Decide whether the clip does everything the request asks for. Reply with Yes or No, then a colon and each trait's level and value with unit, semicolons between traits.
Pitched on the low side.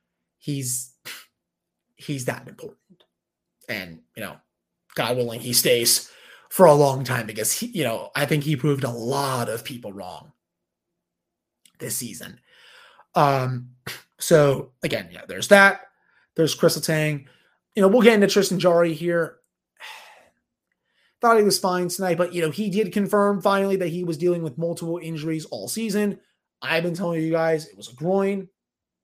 No: medium, 165 Hz